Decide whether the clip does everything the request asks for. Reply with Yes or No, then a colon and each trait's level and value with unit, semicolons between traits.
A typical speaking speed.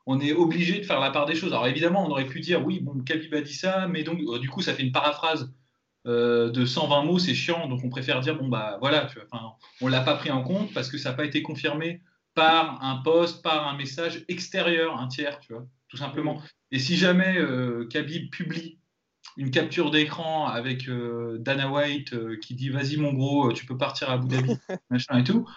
No: fast, 230 wpm